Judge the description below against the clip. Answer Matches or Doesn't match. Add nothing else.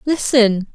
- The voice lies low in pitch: Doesn't match